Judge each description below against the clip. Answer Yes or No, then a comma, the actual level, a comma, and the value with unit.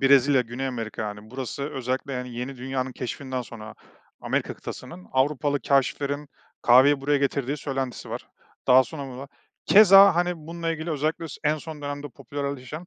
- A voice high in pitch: No, low, 135 Hz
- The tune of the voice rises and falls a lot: No, narrow, 2.5 semitones